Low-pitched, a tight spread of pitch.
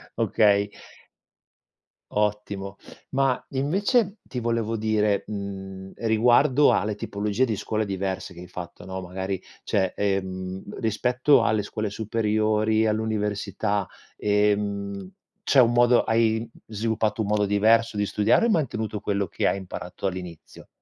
Yes: low, 105 Hz; narrow, 2.3 semitones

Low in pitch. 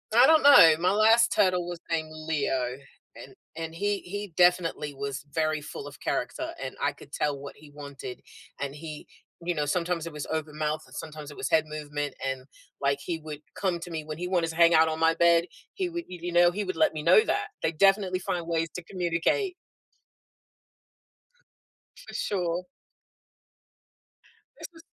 No: medium, 165 Hz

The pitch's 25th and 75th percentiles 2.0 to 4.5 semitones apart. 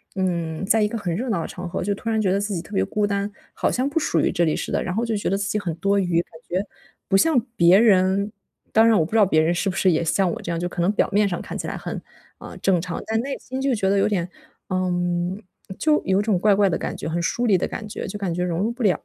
Yes: average, 3.3 semitones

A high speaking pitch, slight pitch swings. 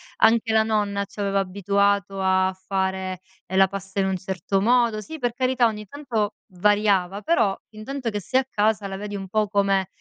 Yes: high, 200 Hz; narrow, 2.3 semitones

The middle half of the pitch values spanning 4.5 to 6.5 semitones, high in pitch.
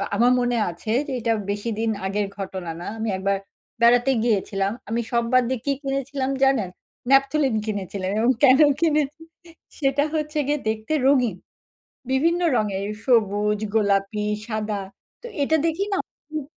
Yes: average, 4.8 semitones; high, 235 Hz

